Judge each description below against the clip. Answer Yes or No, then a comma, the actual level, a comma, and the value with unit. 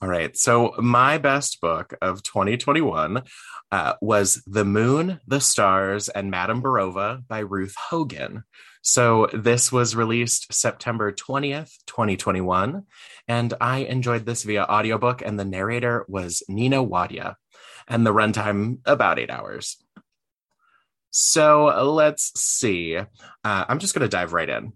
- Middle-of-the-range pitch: No, low, 115 Hz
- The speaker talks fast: No, slow, 135 wpm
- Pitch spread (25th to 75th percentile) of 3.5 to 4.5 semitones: Yes, average, 4.0 semitones